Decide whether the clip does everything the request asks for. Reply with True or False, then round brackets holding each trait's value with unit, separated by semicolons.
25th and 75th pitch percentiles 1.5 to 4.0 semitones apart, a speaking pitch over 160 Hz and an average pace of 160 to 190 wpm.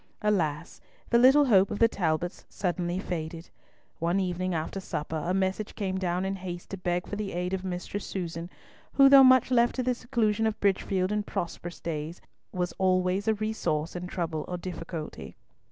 True (3.1 semitones; 185 Hz; 180 wpm)